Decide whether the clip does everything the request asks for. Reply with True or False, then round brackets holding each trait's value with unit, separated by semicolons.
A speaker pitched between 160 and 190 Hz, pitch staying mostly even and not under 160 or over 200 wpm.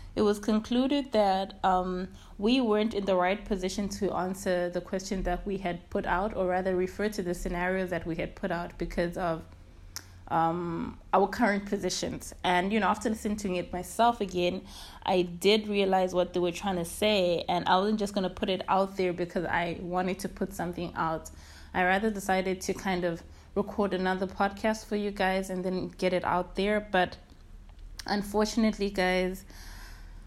True (185 Hz; 2.3 semitones; 185 wpm)